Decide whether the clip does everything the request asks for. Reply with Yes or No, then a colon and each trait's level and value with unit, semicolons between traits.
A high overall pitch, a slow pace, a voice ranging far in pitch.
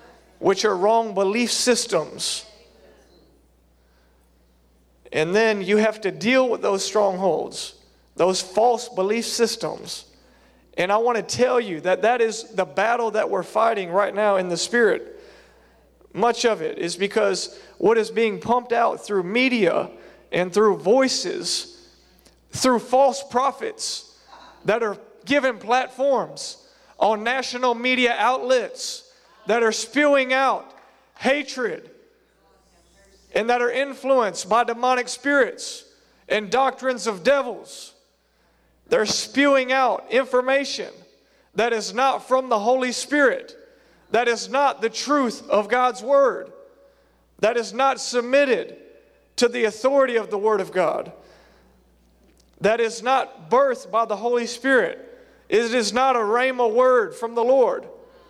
No: high, 245 Hz; slow, 130 wpm; average, 4.1 semitones